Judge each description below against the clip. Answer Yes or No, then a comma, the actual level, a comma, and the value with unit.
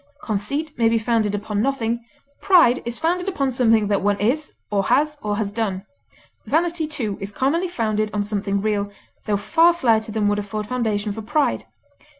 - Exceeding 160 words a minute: Yes, average, 175 wpm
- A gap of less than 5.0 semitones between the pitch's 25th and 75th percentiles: No, average, 5.3 semitones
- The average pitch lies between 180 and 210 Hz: No, high, 225 Hz